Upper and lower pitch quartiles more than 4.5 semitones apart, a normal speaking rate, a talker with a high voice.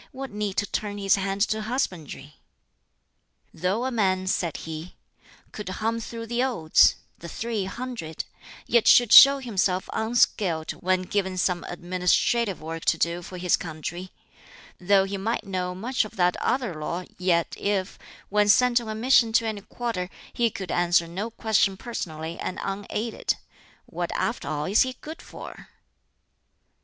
No: average, 4.2 semitones; average, 155 wpm; high, 195 Hz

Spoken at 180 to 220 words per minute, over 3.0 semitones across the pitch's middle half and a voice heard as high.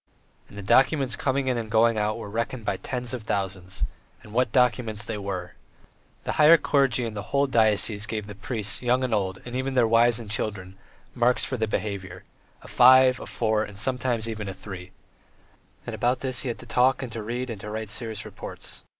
No: fast, 205 wpm; average, 3.4 semitones; low, 115 Hz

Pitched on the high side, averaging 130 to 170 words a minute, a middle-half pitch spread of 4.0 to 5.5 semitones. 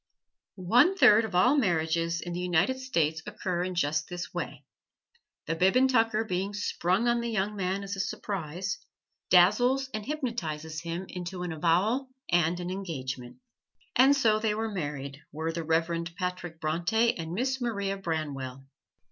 No: medium, 180 Hz; average, 160 wpm; average, 5.0 semitones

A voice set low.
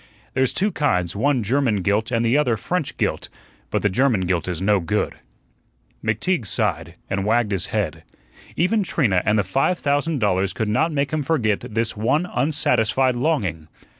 Yes: low, 115 Hz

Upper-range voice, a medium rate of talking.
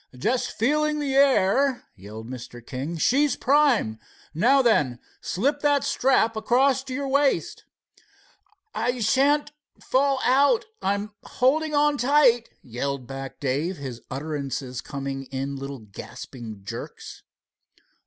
No: high, 225 Hz; slow, 115 wpm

